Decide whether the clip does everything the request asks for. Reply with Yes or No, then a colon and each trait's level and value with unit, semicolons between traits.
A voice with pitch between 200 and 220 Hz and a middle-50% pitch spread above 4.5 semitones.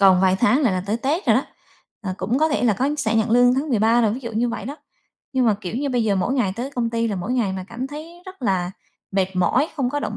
No: high, 235 Hz; average, 4.9 semitones